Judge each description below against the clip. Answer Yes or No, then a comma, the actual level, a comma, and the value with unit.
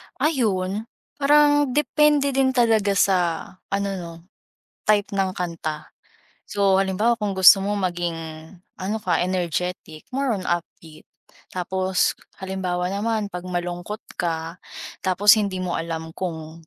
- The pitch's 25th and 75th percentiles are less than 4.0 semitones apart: Yes, average, 3.3 semitones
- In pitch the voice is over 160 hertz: Yes, high, 190 Hz